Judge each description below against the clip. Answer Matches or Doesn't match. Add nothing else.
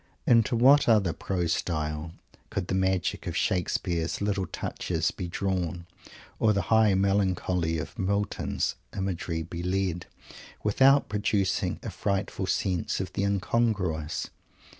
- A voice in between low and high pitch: Doesn't match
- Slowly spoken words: Matches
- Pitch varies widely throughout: Doesn't match